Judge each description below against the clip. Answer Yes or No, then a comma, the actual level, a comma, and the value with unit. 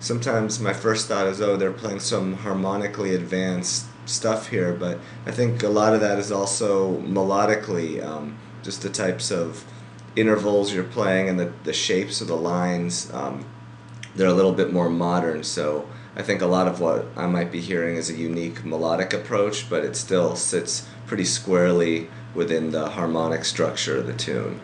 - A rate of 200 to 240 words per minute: No, average, 180 wpm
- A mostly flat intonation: No, average, 3.6 semitones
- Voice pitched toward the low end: Yes, very low, 90 Hz